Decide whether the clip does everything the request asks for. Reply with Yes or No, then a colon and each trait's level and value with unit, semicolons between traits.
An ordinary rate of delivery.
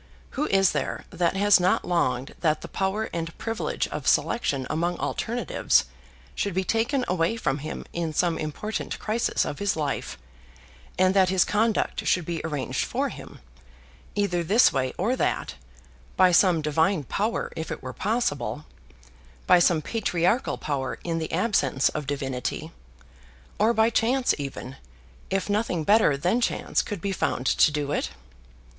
Yes: average, 155 wpm